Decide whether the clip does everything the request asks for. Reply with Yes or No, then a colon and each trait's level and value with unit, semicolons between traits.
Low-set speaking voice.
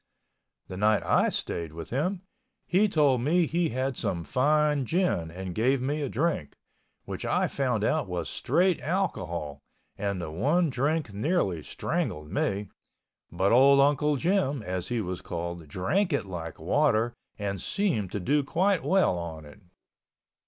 Yes: low, 125 Hz